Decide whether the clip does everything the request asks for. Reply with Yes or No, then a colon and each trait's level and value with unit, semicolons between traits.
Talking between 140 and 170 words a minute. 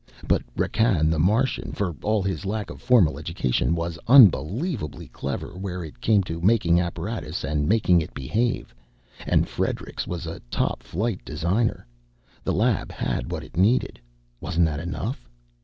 Yes: average, 155 wpm